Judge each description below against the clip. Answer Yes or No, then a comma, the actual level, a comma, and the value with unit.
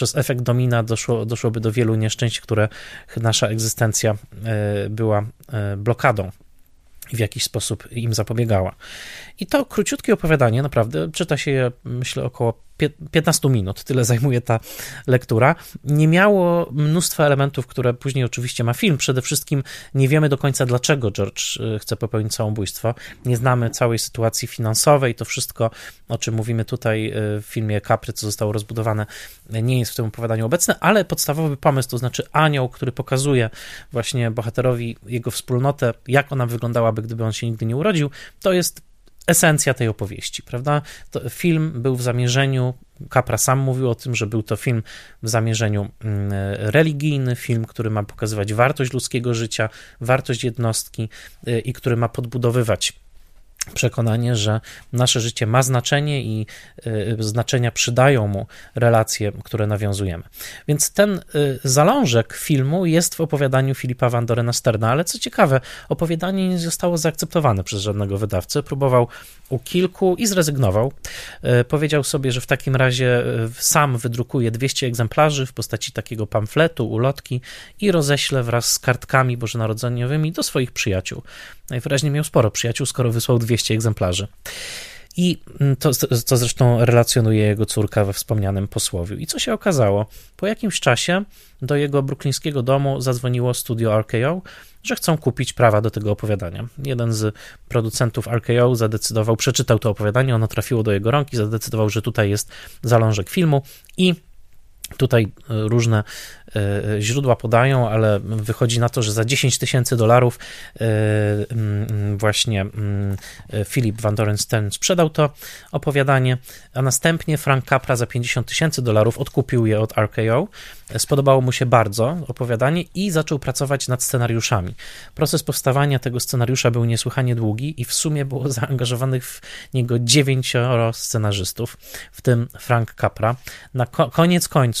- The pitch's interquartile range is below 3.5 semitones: No, average, 3.8 semitones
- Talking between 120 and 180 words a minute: Yes, average, 145 wpm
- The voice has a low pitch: Yes, low, 120 Hz